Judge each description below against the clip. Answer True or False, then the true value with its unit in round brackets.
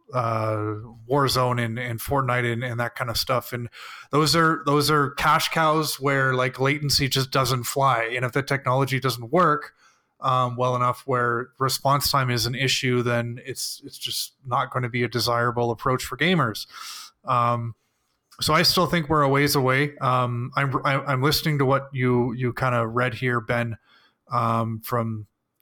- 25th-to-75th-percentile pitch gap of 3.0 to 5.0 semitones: False (2.6 semitones)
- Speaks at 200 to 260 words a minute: False (180 wpm)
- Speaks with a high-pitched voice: False (125 Hz)